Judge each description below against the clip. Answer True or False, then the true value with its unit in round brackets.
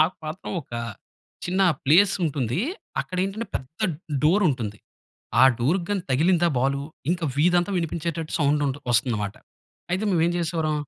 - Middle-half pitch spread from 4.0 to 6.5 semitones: True (4.3 semitones)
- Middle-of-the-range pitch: True (160 Hz)